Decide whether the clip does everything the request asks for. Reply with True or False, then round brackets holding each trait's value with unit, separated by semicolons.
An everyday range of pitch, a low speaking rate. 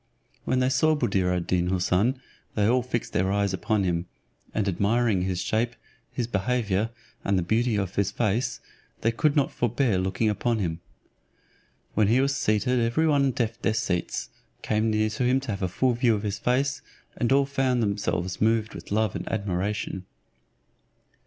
False (4.0 semitones; 170 wpm)